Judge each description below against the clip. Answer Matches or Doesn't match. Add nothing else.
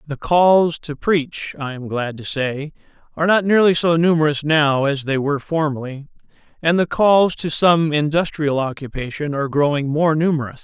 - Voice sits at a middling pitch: Matches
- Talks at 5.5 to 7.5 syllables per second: Doesn't match